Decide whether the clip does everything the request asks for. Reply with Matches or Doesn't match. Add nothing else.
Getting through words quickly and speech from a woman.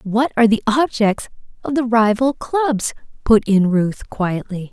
Doesn't match